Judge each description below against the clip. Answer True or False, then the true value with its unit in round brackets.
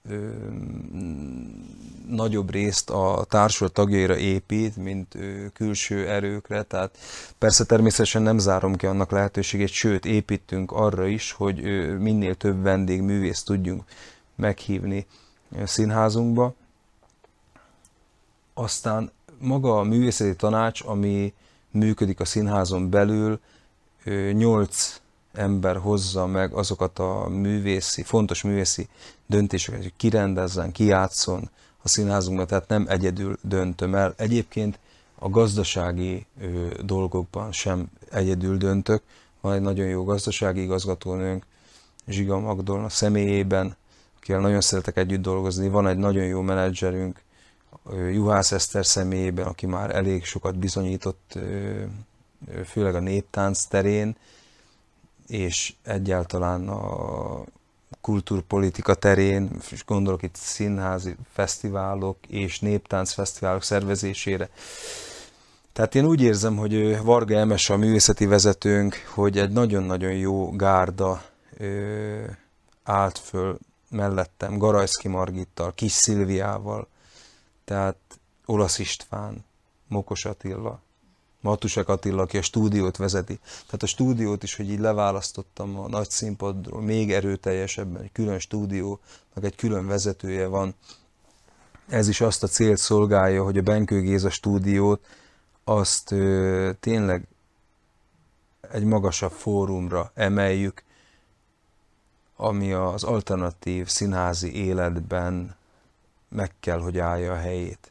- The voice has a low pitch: True (100 Hz)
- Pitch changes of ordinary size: False (2.0 semitones)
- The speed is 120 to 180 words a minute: False (105 wpm)